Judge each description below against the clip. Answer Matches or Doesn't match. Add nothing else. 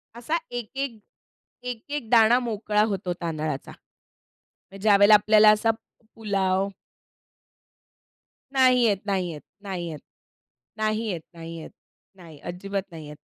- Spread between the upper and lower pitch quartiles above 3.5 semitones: Matches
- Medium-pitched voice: Doesn't match